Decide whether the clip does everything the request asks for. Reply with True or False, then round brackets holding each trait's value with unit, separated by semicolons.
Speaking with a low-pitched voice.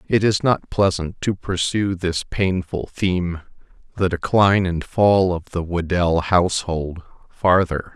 True (90 Hz)